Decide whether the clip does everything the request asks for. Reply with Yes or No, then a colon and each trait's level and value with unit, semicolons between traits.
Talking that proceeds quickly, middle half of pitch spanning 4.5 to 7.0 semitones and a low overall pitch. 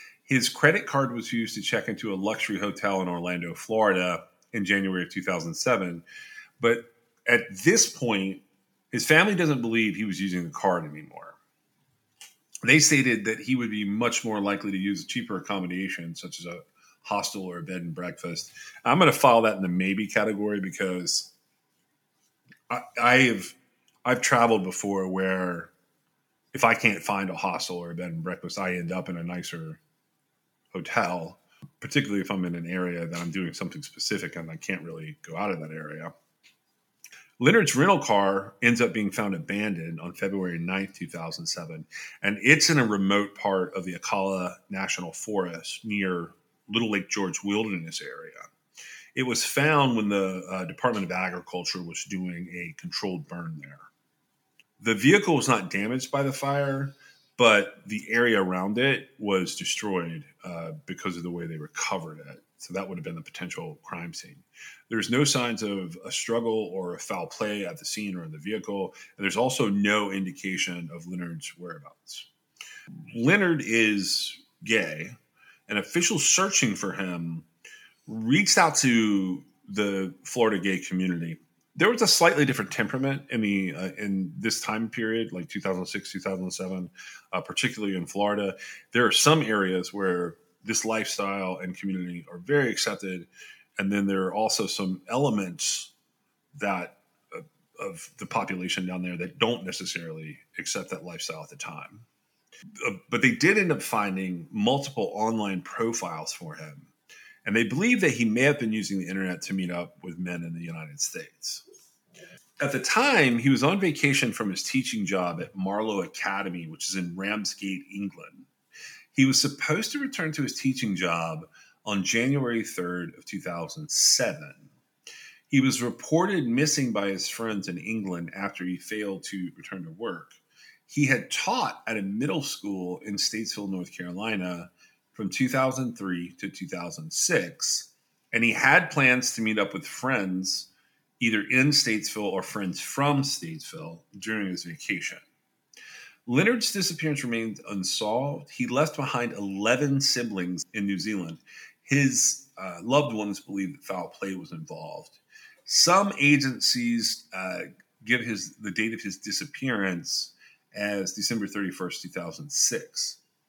No: average, 160 wpm; average, 5.1 semitones; low, 100 Hz